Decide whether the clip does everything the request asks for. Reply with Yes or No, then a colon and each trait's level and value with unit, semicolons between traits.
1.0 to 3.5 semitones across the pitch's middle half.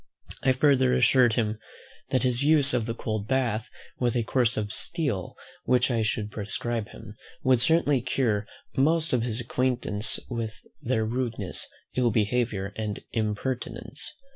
Yes: average, 3.0 semitones